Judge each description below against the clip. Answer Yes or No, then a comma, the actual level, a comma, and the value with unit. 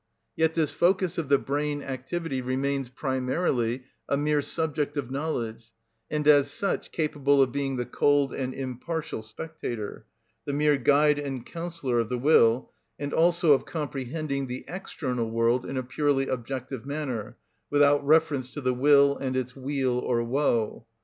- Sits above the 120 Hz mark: Yes, medium, 140 Hz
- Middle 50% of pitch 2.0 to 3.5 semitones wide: Yes, average, 2.8 semitones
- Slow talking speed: No, average, 155 wpm